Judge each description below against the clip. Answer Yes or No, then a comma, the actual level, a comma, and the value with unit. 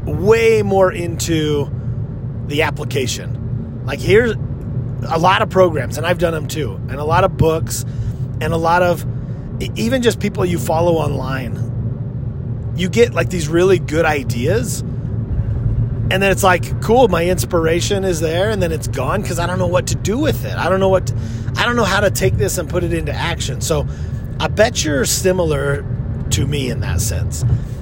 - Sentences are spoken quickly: No, average, 190 wpm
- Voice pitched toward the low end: Yes, low, 130 Hz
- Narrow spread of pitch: No, average, 4.5 semitones